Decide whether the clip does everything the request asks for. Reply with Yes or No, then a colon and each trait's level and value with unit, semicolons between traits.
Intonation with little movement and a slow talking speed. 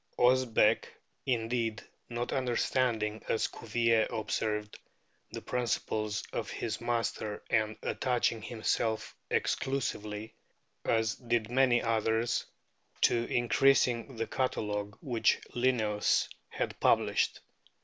Yes: narrow, 2.0 semitones; slow, 95 wpm